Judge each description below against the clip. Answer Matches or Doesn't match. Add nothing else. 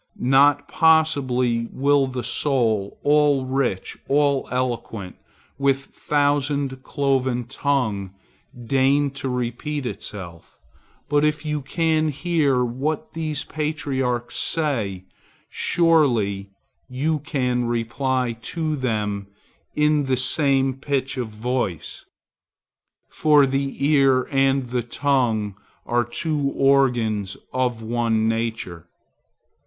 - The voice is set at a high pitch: Doesn't match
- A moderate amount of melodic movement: Matches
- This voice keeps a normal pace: Doesn't match